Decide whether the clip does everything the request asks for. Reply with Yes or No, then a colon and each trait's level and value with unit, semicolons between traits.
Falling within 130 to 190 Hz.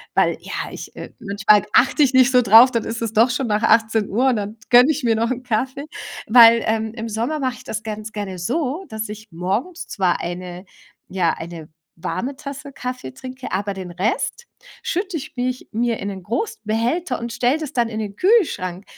No: high, 230 Hz